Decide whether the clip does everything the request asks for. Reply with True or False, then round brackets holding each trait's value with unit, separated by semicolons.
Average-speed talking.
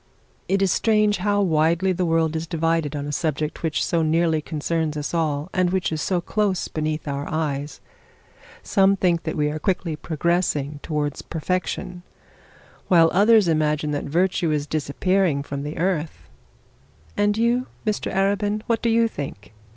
True (160 wpm)